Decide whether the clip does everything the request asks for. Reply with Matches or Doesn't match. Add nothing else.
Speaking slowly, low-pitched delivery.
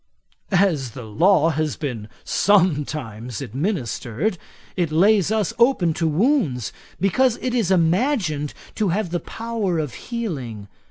Doesn't match